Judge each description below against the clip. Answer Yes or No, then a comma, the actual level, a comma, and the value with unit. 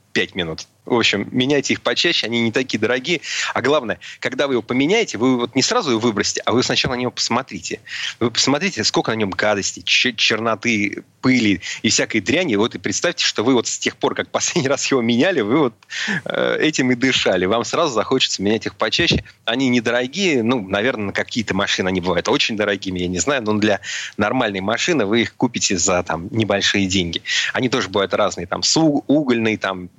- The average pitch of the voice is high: No, low, 110 Hz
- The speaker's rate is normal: No, fast, 200 wpm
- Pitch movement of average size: Yes, average, 4.3 semitones